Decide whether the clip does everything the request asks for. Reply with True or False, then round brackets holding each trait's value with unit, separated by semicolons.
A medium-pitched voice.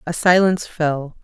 True (165 Hz)